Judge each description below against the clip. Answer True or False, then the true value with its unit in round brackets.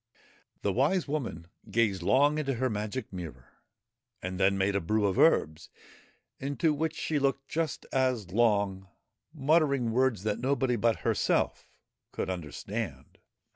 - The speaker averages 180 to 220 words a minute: False (135 wpm)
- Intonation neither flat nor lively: False (6.0 semitones)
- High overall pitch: False (115 Hz)